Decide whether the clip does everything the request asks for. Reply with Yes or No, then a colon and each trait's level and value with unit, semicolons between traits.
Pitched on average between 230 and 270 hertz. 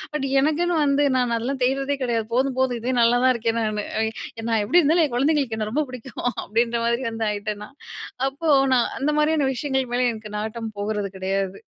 Yes: high, 245 Hz